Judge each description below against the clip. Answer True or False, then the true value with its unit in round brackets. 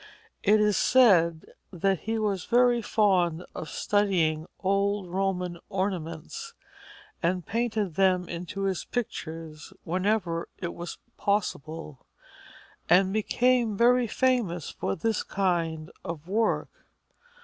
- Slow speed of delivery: True (110 wpm)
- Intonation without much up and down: False (4.1 semitones)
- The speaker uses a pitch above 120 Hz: True (190 Hz)